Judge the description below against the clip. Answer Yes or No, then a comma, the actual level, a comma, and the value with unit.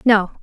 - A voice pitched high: Yes, high, 210 Hz